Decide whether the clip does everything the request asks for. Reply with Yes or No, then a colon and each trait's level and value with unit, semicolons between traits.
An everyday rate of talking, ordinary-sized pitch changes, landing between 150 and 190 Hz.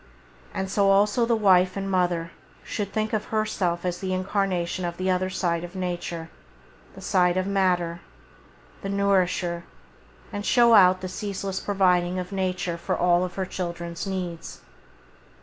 No: average, 160 wpm; narrow, 2.0 semitones; medium, 185 Hz